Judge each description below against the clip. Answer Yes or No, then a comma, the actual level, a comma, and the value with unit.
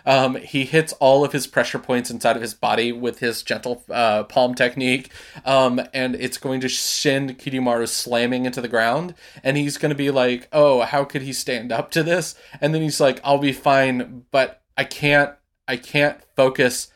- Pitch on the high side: No, low, 130 Hz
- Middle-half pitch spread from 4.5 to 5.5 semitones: No, narrow, 2.6 semitones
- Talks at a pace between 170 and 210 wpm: Yes, average, 200 wpm